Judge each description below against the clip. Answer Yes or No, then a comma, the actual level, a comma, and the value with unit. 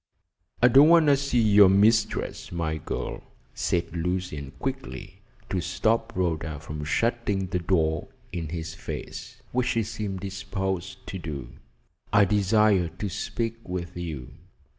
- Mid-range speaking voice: No, very low, 95 Hz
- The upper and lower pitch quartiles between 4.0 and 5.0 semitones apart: Yes, average, 4.6 semitones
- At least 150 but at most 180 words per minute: No, average, 140 wpm